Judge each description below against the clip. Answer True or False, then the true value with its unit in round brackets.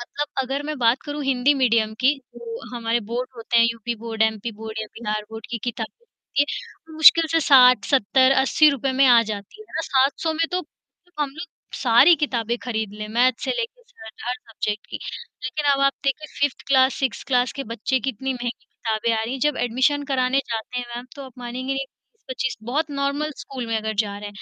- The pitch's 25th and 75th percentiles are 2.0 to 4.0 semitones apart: True (3.4 semitones)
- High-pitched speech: True (255 Hz)